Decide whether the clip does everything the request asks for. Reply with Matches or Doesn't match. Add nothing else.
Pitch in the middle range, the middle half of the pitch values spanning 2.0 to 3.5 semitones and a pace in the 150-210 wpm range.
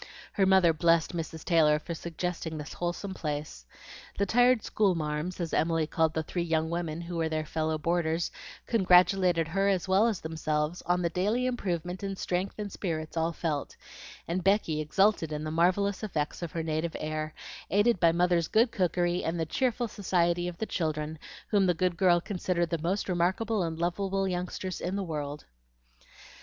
Matches